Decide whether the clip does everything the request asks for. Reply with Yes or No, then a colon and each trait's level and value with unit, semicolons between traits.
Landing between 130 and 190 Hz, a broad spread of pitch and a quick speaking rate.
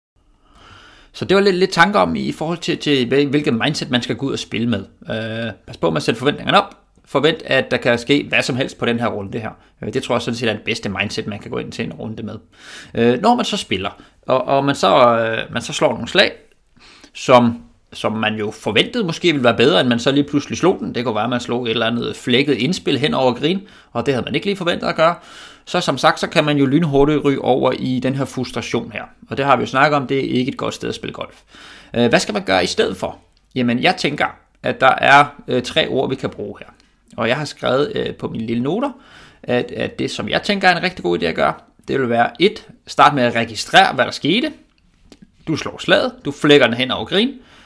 Yes: low, 135 Hz; wide, 5.9 semitones; fast, 260 wpm